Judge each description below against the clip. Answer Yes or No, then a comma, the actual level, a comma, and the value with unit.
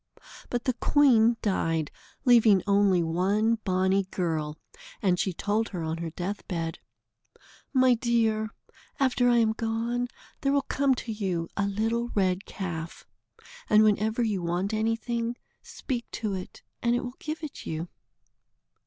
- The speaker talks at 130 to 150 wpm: Yes, average, 145 wpm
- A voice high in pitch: Yes, high, 215 Hz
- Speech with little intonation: No, average, 4.4 semitones